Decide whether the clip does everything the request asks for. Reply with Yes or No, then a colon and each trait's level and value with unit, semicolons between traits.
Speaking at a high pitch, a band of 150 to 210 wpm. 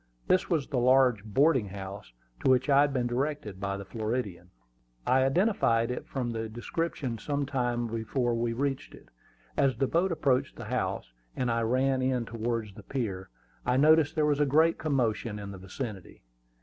No: low, 125 Hz; average, 180 wpm